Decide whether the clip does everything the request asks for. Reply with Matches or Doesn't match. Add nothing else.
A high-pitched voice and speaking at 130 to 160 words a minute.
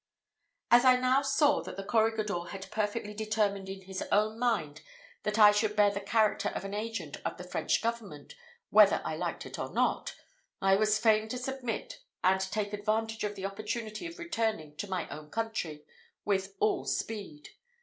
Doesn't match